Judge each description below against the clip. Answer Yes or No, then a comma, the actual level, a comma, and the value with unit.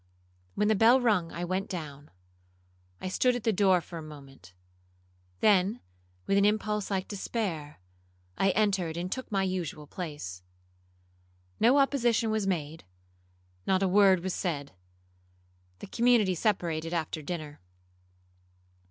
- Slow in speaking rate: Yes, slow, 125 wpm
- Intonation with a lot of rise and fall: Yes, wide, 6.0 semitones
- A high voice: No, medium, 180 Hz